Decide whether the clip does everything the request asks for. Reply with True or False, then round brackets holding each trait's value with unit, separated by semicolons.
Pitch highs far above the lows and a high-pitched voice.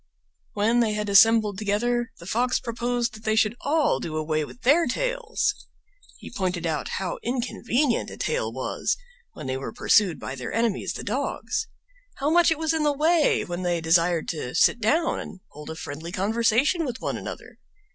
True (6.8 semitones; 225 Hz)